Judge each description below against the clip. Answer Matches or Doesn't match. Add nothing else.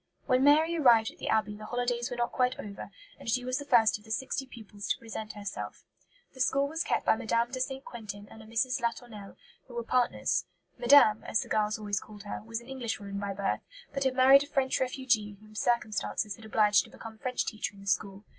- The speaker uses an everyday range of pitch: Matches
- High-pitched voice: Matches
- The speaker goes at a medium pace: Doesn't match